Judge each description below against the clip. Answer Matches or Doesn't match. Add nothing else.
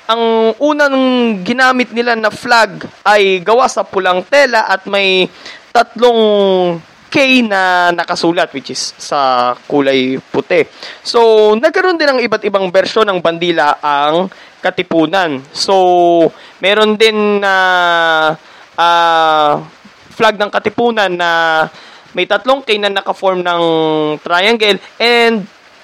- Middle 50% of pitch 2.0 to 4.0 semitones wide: Doesn't match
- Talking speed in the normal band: Matches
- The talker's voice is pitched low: Doesn't match